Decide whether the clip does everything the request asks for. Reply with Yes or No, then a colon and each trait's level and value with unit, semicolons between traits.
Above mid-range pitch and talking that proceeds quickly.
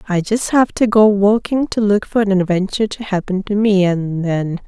Yes: high, 200 Hz; fast, 220 wpm